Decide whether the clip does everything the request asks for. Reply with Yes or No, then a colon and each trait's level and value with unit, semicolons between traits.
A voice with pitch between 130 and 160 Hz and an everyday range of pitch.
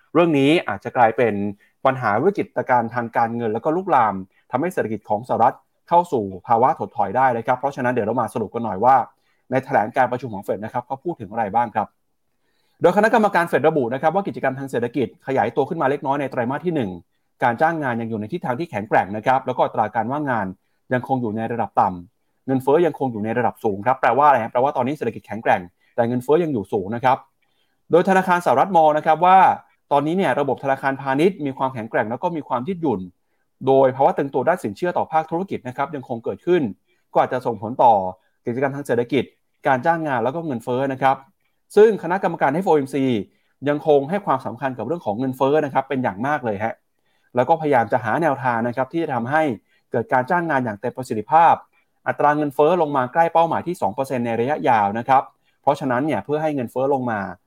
Yes: low, 135 Hz; average, 4.5 semitones